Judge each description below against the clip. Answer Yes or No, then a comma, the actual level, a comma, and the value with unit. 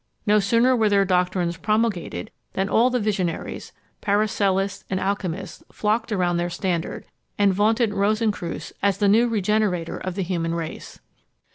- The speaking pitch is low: No, high, 200 Hz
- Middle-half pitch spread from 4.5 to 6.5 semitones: No, average, 2.9 semitones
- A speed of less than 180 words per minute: Yes, average, 145 wpm